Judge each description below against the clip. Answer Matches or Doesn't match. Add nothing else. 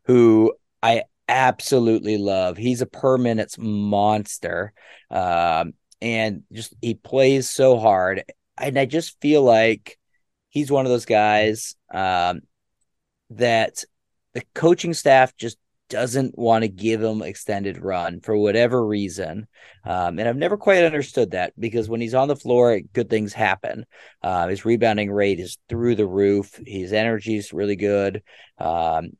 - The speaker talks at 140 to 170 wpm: Matches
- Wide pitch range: Doesn't match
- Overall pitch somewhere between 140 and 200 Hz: Doesn't match